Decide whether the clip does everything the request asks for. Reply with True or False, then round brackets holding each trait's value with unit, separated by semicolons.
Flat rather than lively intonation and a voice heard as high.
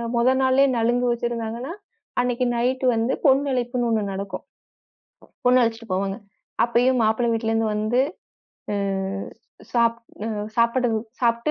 True (1.8 semitones; 235 Hz)